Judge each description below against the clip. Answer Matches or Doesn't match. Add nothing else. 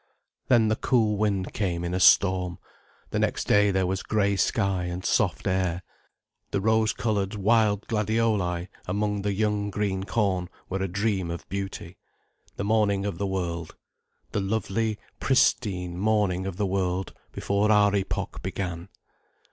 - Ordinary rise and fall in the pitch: Doesn't match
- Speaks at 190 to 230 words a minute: Doesn't match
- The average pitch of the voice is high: Doesn't match